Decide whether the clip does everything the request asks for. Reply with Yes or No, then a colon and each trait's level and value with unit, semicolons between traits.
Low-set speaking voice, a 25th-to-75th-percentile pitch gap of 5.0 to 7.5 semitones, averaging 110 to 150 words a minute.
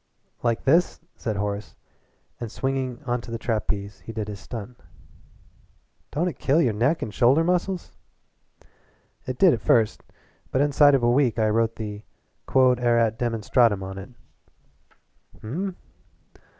No: low, 120 Hz; average, 4.0 semitones; average, 140 wpm